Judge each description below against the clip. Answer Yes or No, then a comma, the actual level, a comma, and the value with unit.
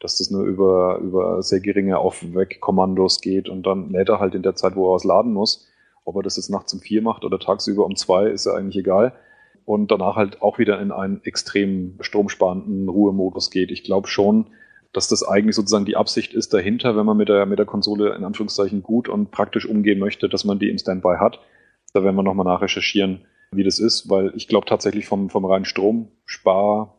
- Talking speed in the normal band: No, fast, 215 wpm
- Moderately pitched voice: No, low, 100 Hz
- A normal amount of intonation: No, narrow, 1.6 semitones